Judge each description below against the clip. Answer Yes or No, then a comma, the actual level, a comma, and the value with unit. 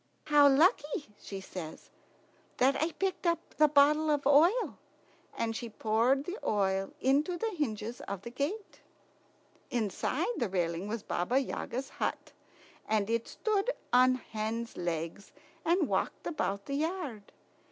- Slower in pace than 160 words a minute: Yes, average, 140 wpm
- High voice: Yes, very high, 255 Hz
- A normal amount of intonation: No, wide, 6.3 semitones